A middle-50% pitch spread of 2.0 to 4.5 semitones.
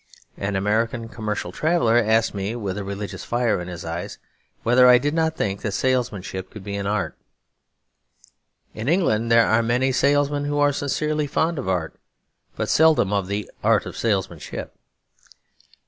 No: wide, 5.6 semitones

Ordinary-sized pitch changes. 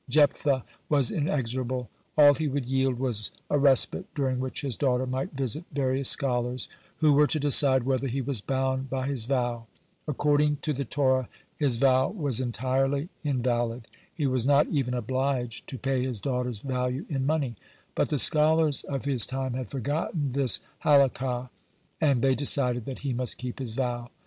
No: narrow, 2.1 semitones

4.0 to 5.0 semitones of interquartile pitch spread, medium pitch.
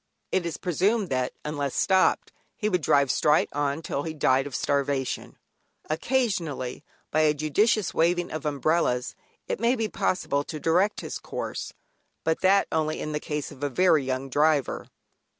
Yes: average, 4.3 semitones; medium, 155 Hz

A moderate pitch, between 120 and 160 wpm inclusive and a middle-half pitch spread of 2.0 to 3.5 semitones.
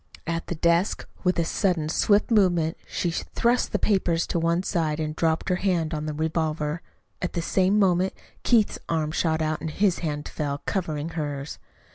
No: medium, 165 Hz; average, 180 wpm; average, 2.8 semitones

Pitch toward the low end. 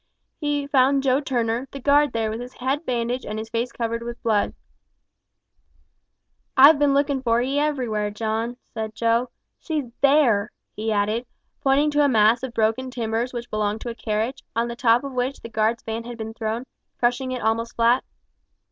No: high, 240 Hz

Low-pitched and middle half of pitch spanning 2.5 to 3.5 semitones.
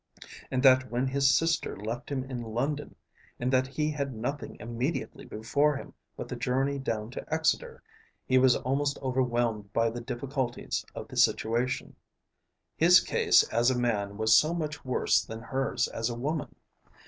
Yes: low, 130 Hz; average, 3.1 semitones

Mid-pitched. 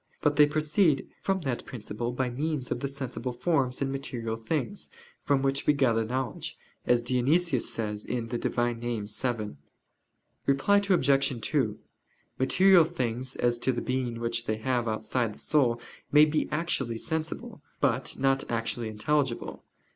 No: low, 130 Hz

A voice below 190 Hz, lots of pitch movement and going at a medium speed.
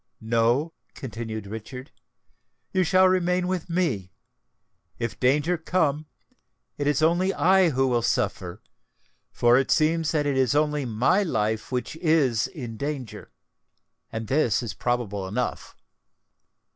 No: low, 135 Hz; wide, 5.8 semitones; slow, 125 wpm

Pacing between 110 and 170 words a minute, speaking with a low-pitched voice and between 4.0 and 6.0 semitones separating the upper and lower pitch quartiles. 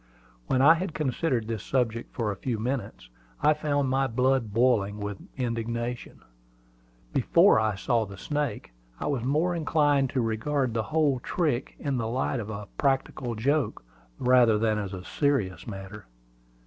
Yes: average, 160 wpm; low, 125 Hz; average, 4.3 semitones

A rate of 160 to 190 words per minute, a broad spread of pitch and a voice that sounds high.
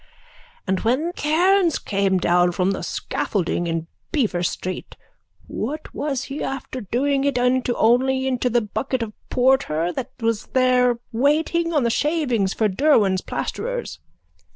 No: average, 145 wpm; wide, 5.8 semitones; very high, 250 Hz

